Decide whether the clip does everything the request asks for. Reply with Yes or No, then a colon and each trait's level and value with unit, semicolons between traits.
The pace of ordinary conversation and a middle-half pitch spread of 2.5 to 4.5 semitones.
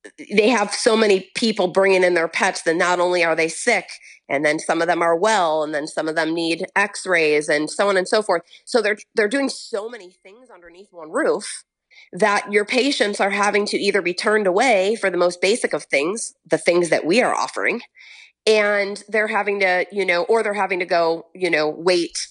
No: fast, 220 wpm; average, 3.4 semitones